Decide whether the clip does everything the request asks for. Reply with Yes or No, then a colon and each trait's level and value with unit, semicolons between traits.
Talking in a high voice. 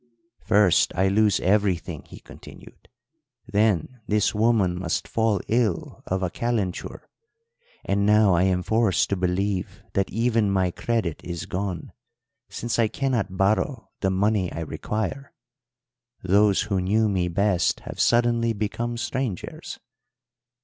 No: low, 100 Hz